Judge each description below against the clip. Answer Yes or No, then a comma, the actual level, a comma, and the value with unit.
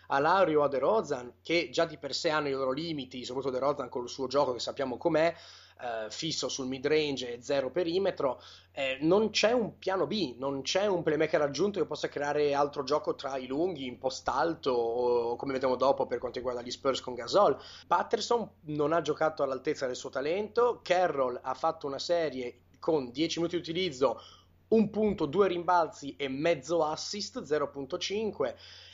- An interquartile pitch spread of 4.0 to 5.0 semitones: Yes, average, 4.4 semitones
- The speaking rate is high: Yes, fast, 185 wpm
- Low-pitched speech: No, medium, 150 Hz